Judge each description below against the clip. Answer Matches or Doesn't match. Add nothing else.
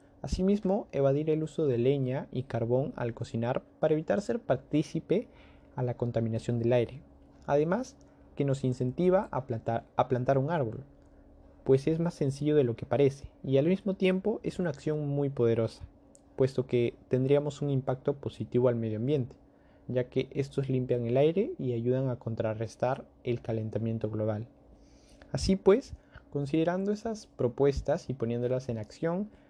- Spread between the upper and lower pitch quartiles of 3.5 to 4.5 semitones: Matches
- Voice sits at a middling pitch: Doesn't match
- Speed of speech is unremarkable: Matches